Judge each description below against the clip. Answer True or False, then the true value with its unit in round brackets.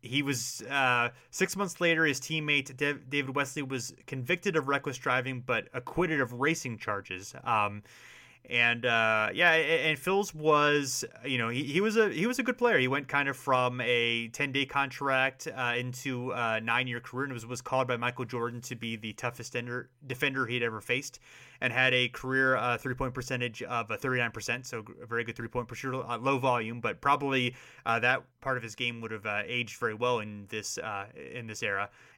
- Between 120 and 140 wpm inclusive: False (200 wpm)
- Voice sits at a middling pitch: False (125 Hz)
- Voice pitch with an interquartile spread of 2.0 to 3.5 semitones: True (2.8 semitones)